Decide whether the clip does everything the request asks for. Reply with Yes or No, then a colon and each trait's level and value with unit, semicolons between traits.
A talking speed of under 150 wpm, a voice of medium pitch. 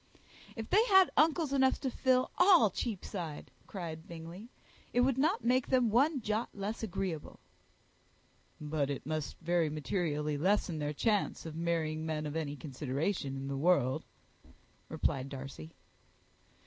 Yes: average, 140 wpm; medium, 170 Hz